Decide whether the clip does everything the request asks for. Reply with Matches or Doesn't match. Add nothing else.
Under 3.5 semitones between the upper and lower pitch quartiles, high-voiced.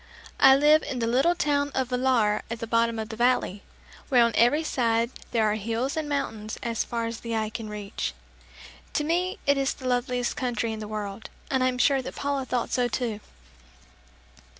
Matches